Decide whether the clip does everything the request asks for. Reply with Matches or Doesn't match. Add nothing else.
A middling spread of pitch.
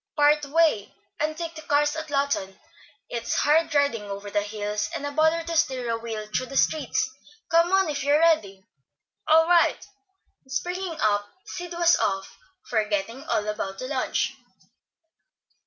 Doesn't match